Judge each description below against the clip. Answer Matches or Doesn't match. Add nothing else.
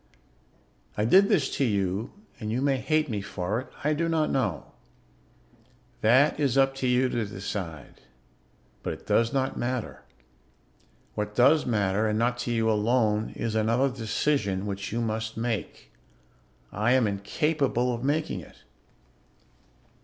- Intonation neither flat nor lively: Matches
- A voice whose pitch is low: Matches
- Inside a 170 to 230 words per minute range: Doesn't match